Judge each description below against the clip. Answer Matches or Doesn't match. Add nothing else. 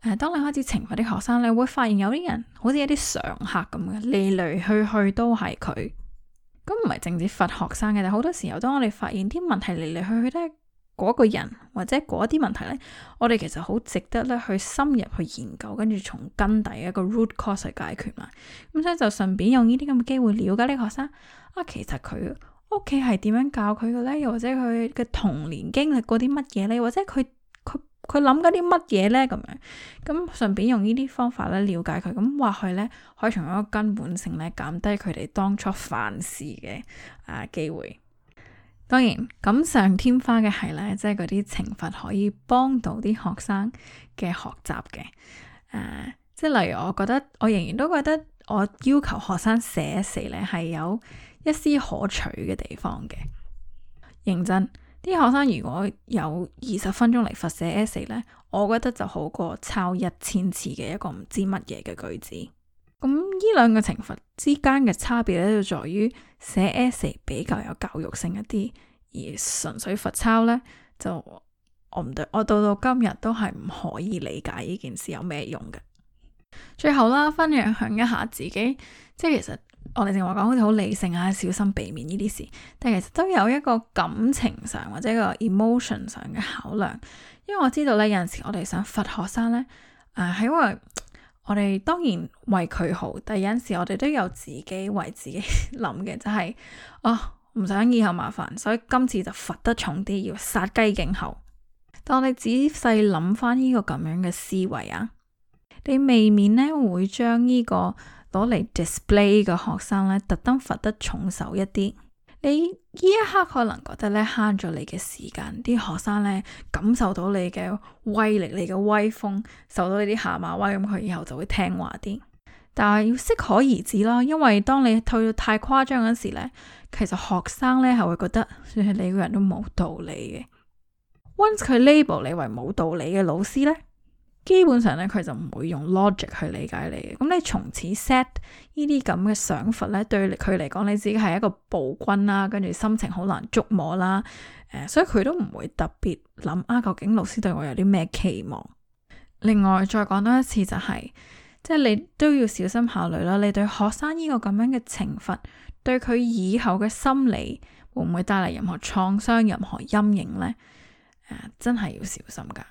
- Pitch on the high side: Matches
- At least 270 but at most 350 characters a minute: Matches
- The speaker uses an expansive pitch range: Doesn't match